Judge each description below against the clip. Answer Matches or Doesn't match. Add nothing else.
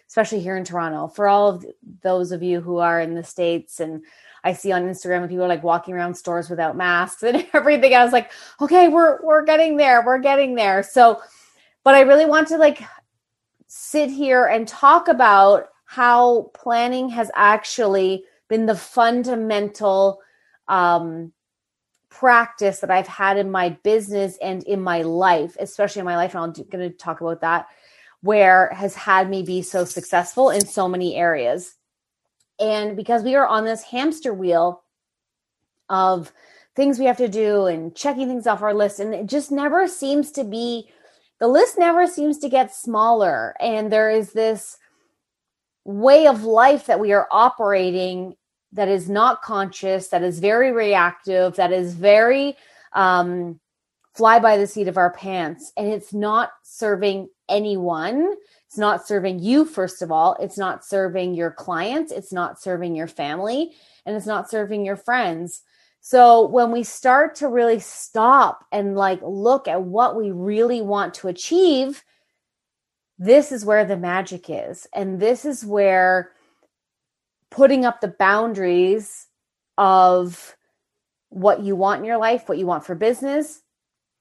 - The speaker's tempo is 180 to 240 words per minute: Doesn't match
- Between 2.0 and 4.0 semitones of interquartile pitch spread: Doesn't match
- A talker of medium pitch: Doesn't match